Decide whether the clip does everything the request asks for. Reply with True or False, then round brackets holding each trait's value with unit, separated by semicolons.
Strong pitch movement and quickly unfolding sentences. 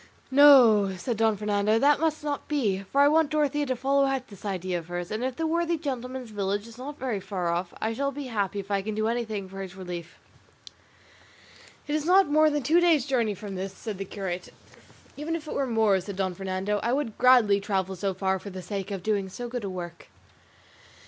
True (6.3 semitones; 220 wpm)